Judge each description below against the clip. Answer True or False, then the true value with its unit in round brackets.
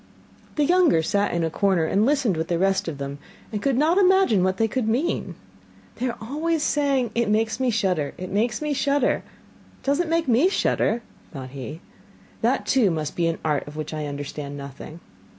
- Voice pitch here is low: False (210 Hz)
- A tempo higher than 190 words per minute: True (205 wpm)